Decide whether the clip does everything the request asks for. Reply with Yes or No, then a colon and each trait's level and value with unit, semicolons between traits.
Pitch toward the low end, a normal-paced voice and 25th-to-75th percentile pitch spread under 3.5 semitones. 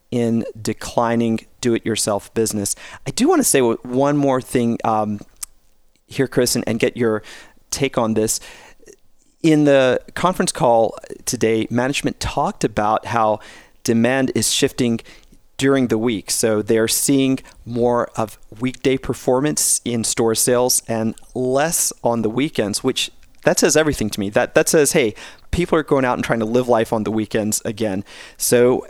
Yes: low, 115 Hz; average, 160 wpm; narrow, 2.6 semitones